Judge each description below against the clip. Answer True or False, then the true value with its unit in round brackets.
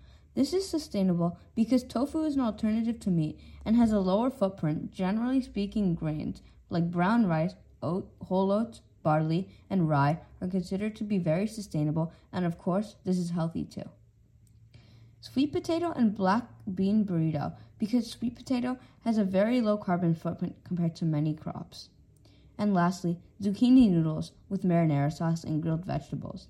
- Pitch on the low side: False (190 Hz)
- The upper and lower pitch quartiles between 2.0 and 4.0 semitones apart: False (5.5 semitones)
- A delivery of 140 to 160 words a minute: True (155 wpm)